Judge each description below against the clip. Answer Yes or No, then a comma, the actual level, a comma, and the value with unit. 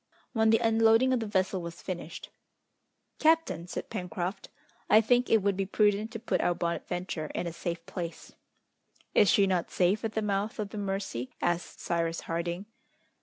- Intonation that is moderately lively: Yes, average, 4.1 semitones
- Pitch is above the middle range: Yes, high, 195 Hz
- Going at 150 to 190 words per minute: Yes, average, 170 wpm